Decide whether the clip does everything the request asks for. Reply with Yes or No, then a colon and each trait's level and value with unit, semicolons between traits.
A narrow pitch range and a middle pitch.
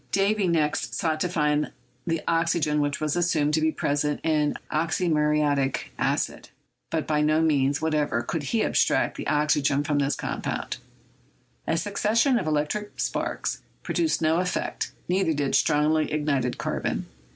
Yes: narrow, 2.2 semitones; medium, 155 Hz